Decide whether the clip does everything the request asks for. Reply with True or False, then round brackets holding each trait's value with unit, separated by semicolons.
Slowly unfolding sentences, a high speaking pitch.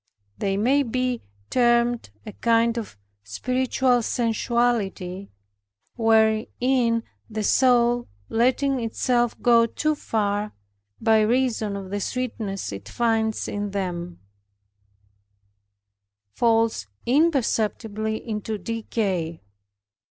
True (90 wpm; 225 Hz)